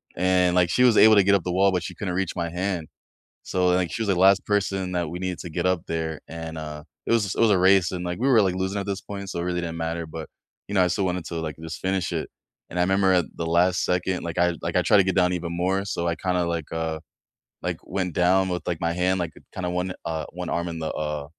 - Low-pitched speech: Yes, very low, 90 Hz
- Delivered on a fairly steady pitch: Yes, narrow, 2.0 semitones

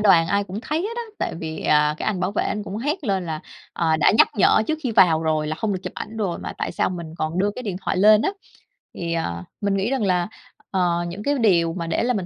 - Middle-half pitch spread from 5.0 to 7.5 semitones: No, average, 4.3 semitones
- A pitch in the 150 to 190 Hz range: Yes, medium, 185 Hz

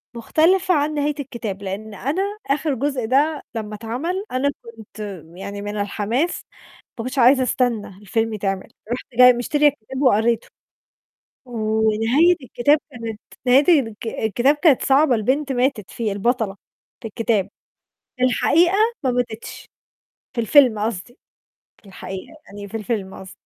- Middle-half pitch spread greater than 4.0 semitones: Yes, average, 4.5 semitones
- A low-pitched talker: No, high, 240 Hz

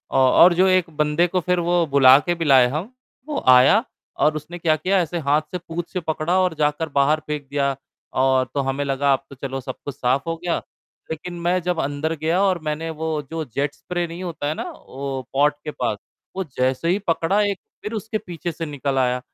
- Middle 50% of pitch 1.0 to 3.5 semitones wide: No, average, 3.9 semitones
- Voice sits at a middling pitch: Yes, medium, 155 Hz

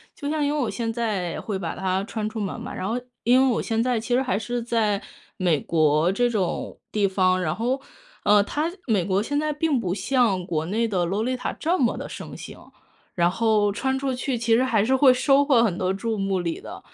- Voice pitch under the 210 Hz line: No, high, 225 Hz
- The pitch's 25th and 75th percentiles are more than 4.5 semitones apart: Yes, average, 4.9 semitones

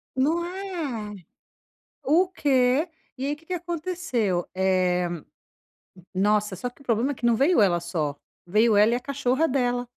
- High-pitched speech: Yes, very high, 250 Hz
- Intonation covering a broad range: Yes, wide, 6.7 semitones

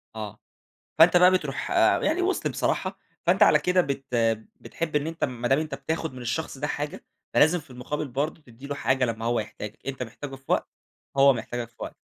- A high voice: No, low, 135 Hz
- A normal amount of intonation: Yes, average, 4.5 semitones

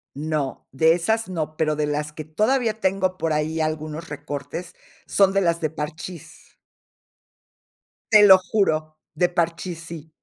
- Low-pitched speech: No, medium, 160 Hz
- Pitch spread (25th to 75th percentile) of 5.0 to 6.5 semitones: No, average, 3.2 semitones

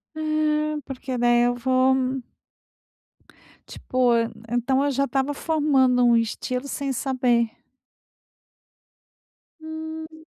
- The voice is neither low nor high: No, very high, 260 Hz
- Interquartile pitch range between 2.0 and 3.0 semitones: Yes, narrow, 2.5 semitones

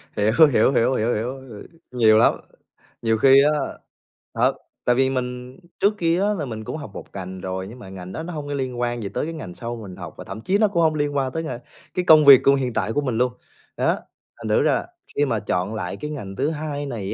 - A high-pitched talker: No, low, 125 Hz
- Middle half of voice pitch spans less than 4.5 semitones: No, average, 5.1 semitones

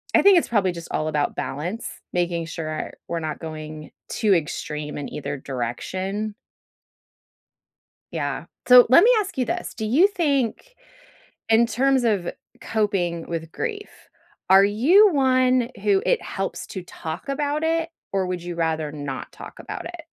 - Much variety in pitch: Yes, wide, 8.7 semitones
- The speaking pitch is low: No, high, 195 Hz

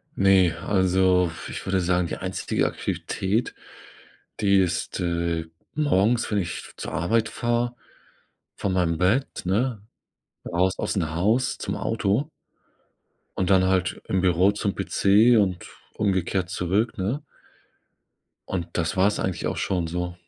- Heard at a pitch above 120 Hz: No, very low, 95 Hz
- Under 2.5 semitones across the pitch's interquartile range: No, average, 2.8 semitones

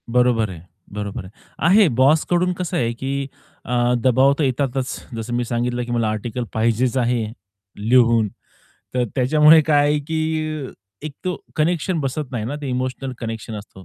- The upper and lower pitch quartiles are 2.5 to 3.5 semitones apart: No, average, 4.3 semitones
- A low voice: Yes, low, 130 Hz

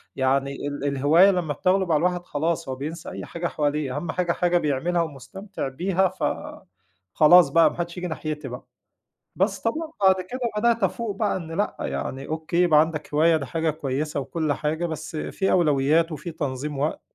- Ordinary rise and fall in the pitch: Yes, average, 3.7 semitones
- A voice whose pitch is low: No, medium, 160 Hz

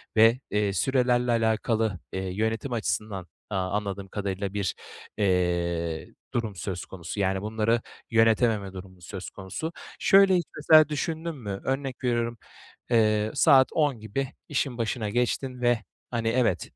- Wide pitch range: No, average, 4.1 semitones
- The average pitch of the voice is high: No, low, 110 Hz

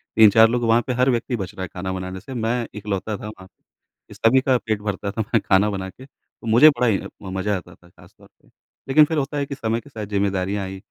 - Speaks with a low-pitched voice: Yes, low, 110 Hz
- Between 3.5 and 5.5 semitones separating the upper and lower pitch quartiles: Yes, average, 4.1 semitones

